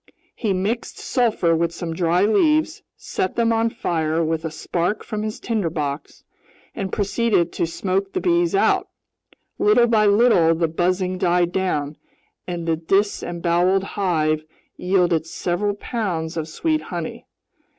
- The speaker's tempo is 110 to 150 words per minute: Yes, average, 140 wpm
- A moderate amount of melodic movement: Yes, average, 4.4 semitones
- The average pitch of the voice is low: No, medium, 185 Hz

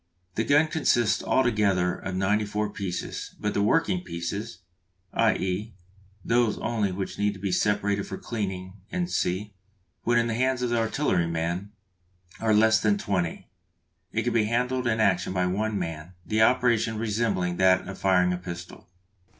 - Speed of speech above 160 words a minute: No, average, 155 wpm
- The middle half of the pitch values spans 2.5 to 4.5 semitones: Yes, average, 3.6 semitones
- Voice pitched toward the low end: Yes, low, 105 Hz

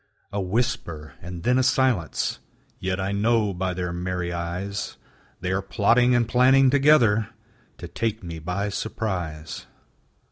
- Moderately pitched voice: No, low, 100 Hz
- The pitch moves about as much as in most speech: Yes, average, 4.7 semitones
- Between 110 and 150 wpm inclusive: Yes, average, 140 wpm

